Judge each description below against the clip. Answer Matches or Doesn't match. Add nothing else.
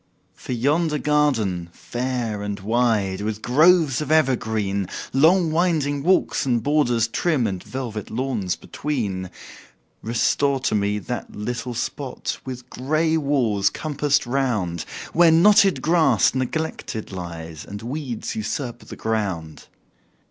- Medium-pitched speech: Doesn't match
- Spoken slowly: Matches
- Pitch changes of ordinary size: Doesn't match